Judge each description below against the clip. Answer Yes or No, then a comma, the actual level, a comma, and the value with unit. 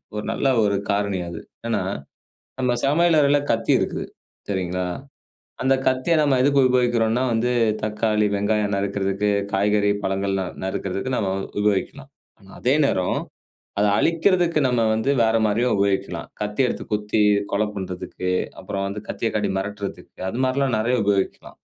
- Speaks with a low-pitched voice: Yes, low, 105 Hz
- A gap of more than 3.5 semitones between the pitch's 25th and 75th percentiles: Yes, average, 4.2 semitones